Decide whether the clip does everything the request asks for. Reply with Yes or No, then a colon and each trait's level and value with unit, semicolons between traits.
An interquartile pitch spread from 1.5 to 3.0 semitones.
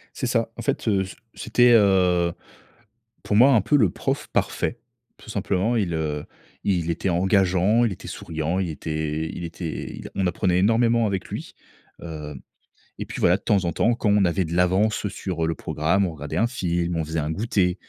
No: average, 3.7 semitones